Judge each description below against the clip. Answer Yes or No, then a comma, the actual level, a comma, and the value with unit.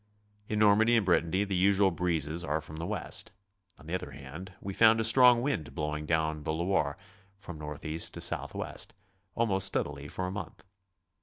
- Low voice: Yes, very low, 90 Hz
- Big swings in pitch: No, average, 4.6 semitones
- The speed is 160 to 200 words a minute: Yes, average, 180 wpm